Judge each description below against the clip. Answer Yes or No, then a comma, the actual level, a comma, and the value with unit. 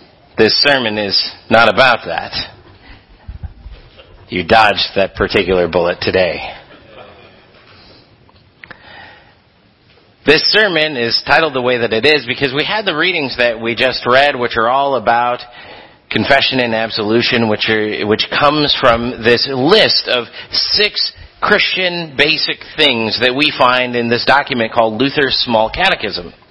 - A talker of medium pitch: No, low, 125 Hz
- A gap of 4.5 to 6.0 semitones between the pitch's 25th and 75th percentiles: No, average, 4.1 semitones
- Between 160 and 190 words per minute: No, slow, 135 wpm